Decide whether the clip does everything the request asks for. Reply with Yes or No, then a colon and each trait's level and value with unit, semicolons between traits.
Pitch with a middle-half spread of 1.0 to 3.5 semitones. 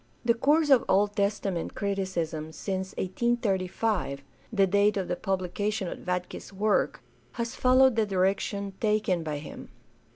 Yes: average, 2.8 semitones